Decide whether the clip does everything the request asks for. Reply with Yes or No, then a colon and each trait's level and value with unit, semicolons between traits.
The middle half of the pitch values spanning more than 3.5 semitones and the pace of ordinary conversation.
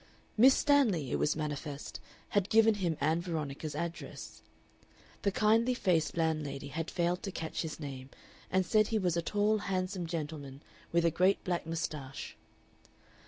Yes: average, 4.5 semitones; average, 155 wpm